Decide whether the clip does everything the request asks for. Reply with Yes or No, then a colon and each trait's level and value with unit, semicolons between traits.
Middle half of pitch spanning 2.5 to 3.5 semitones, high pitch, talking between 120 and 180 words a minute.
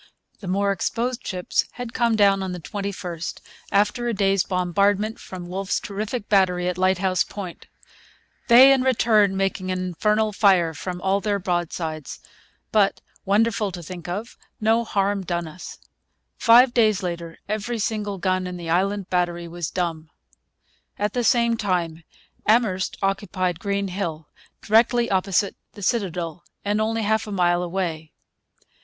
Yes: average, 3.2 semitones; high, 195 Hz; average, 150 wpm